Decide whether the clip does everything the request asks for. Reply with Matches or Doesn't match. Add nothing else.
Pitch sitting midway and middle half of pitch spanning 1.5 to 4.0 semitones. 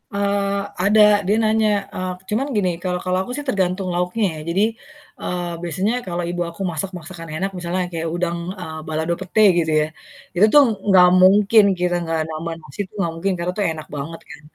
Matches